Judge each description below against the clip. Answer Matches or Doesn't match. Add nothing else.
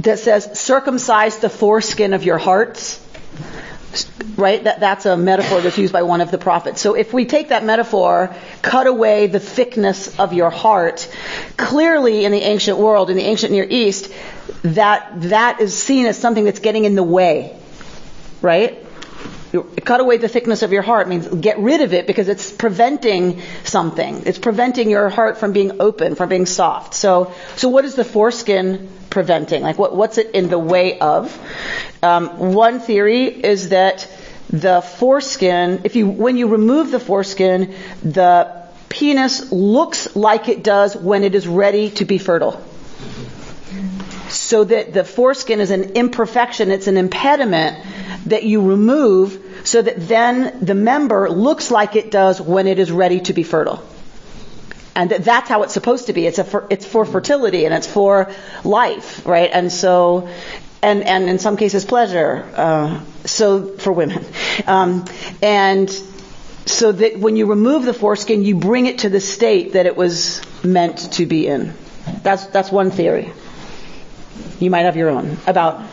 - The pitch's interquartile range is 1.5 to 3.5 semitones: Matches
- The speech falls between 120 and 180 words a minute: Matches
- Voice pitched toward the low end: Doesn't match